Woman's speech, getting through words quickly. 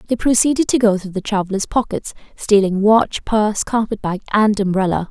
No: female; average, 175 wpm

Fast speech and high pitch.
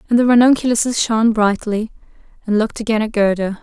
No: average, 165 wpm; high, 220 Hz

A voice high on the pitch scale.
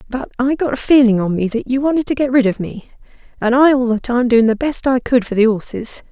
Yes: high, 245 Hz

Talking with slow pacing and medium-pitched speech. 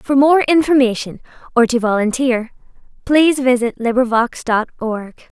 No: slow, 125 wpm; very high, 250 Hz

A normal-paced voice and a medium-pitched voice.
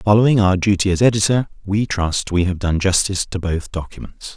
No: average, 195 wpm; very low, 95 Hz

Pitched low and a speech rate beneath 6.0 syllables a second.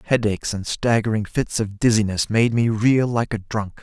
Yes: low, 110 Hz; 5.0 syllables/s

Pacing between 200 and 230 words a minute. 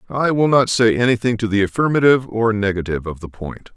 Yes: fast, 205 wpm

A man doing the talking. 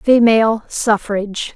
No: female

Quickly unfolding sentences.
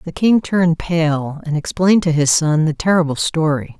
No: average, 190 wpm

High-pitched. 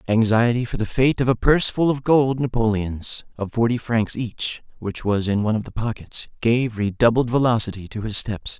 No: low, 115 Hz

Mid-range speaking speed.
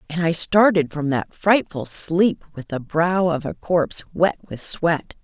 Yes: average, 185 wpm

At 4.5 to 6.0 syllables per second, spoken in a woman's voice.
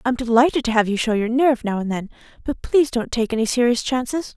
No: 6.7 syllables/s; female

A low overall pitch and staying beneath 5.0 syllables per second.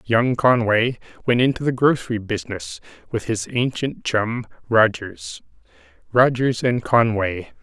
Yes: low, 115 Hz; 4.2 syllables/s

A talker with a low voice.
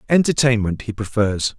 Yes: low, 115 Hz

